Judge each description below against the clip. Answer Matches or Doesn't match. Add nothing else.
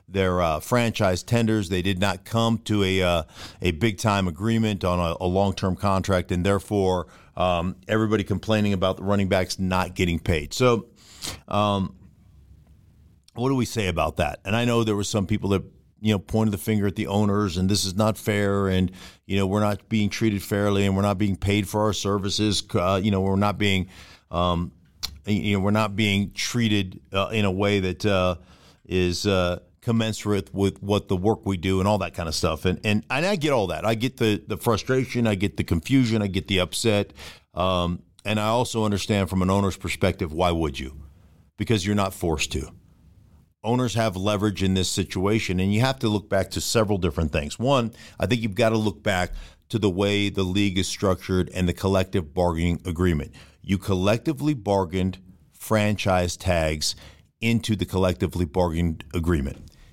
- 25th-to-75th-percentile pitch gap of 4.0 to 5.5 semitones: Doesn't match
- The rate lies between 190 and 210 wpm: Matches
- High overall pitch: Doesn't match